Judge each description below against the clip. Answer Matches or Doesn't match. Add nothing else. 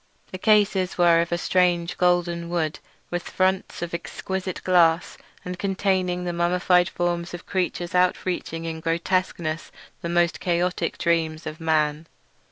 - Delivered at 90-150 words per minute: Matches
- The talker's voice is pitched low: Doesn't match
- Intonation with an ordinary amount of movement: Doesn't match